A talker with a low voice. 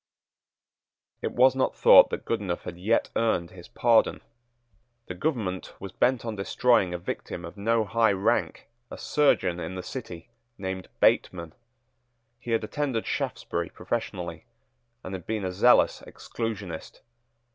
Yes: low, 100 Hz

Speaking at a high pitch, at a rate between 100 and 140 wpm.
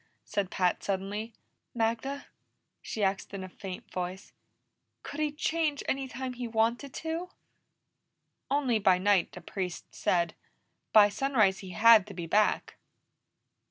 Yes: high, 215 Hz; slow, 135 wpm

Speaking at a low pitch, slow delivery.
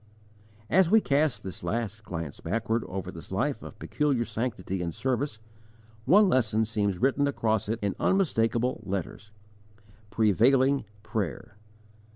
Yes: low, 115 Hz; slow, 130 wpm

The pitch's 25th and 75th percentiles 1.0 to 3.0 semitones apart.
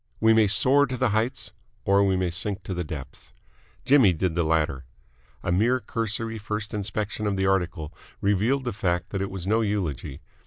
No: average, 3.8 semitones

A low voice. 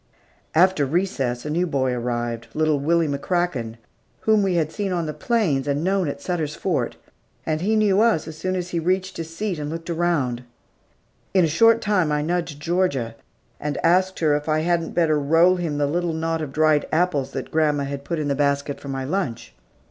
No: medium, 160 Hz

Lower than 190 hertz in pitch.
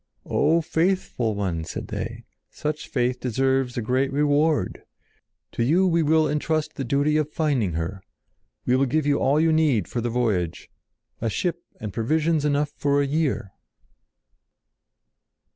Yes: medium, 140 Hz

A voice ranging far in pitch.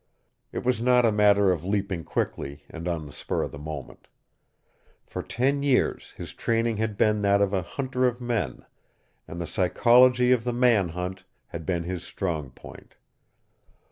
Yes: wide, 5.9 semitones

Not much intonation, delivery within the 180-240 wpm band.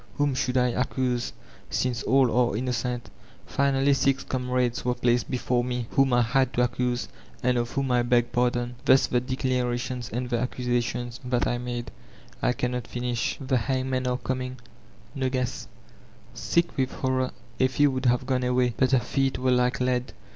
No: narrow, 1.1 semitones; average, 170 wpm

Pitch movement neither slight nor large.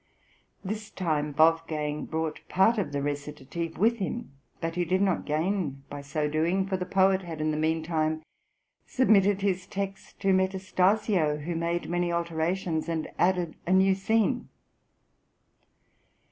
Yes: average, 3.5 semitones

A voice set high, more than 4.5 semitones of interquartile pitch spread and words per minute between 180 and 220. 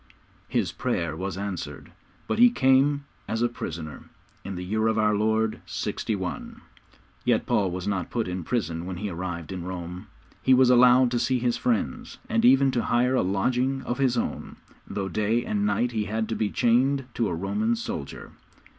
No: low, 110 Hz; average, 5.2 semitones; average, 185 wpm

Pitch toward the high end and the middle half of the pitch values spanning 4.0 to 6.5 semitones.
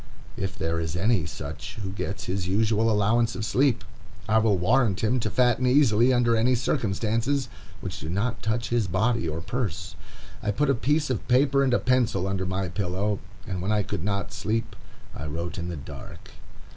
No: low, 105 Hz; average, 4.5 semitones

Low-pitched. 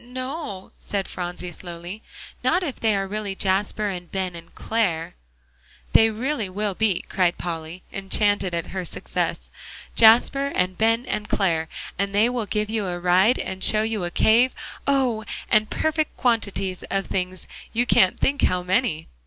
No: high, 200 Hz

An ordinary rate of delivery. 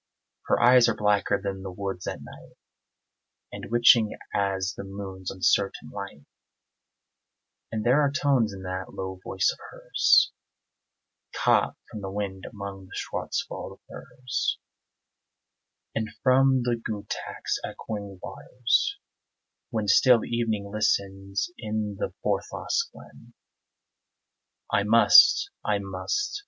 No: slow, 120 wpm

